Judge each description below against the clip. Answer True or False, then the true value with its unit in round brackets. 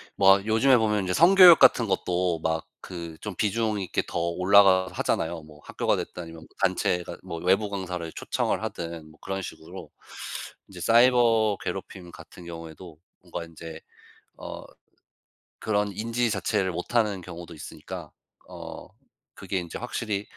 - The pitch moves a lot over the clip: False (4.0 semitones)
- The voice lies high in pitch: False (95 Hz)